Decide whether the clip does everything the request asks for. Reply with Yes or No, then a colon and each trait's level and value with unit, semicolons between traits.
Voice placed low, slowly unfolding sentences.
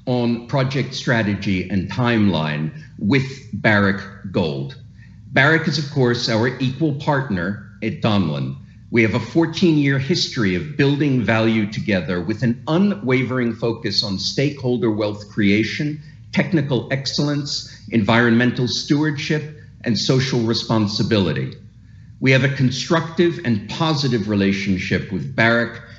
Yes: low, 120 Hz; slow, 120 wpm